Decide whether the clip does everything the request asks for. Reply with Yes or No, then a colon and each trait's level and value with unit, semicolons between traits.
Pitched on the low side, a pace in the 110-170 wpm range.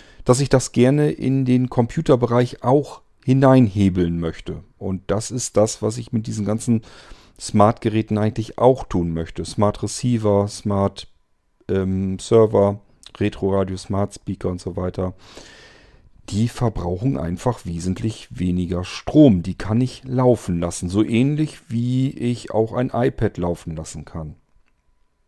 Yes: low, 105 Hz; slow, 125 wpm